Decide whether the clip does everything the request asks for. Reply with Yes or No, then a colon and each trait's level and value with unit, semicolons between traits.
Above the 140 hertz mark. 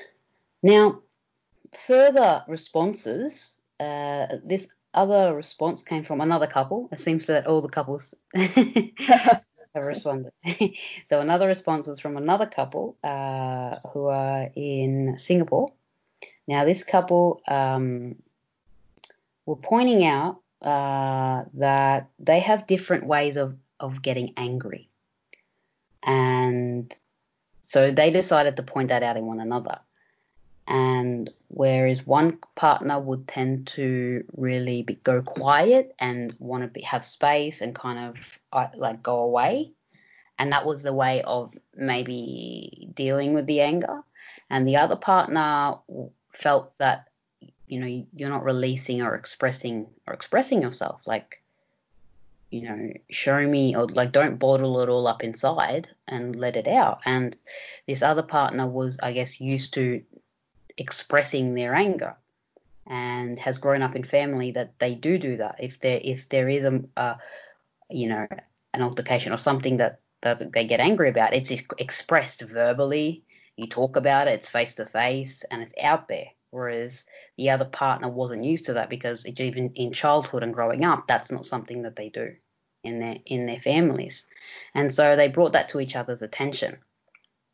No: low, 135 Hz